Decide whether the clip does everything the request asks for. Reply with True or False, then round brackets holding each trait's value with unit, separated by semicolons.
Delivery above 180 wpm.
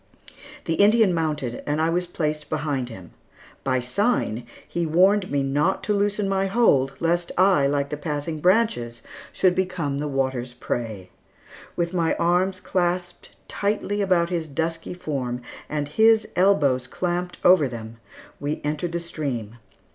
False (145 wpm)